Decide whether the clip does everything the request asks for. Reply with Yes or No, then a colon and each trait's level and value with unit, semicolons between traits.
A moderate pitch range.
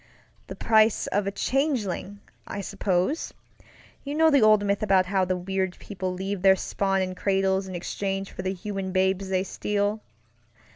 No: narrow, 1.5 semitones